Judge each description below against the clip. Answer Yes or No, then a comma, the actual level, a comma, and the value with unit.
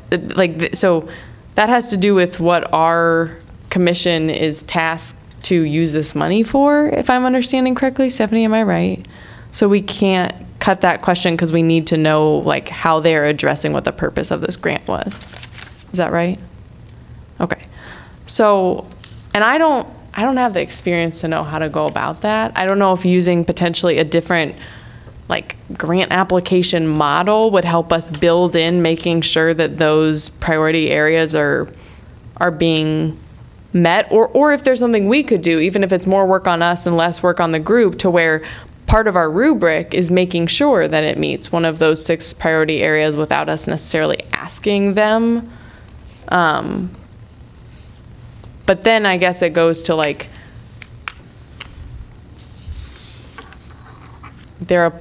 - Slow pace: No, average, 165 wpm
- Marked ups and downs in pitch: No, average, 3.7 semitones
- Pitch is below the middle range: No, medium, 170 Hz